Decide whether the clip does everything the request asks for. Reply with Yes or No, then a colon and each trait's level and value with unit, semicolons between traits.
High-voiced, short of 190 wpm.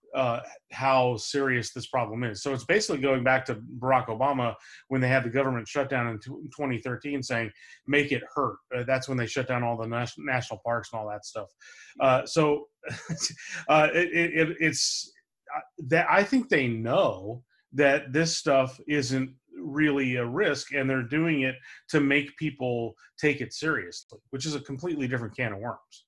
No: low, 130 Hz; average, 180 wpm